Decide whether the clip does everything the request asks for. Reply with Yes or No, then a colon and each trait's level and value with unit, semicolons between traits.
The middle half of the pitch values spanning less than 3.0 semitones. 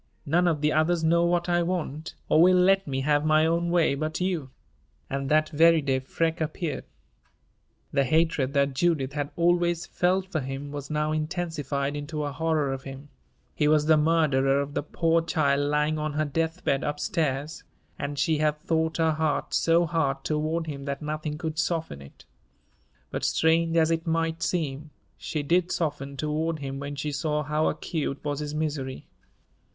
Yes: narrow, 2.4 semitones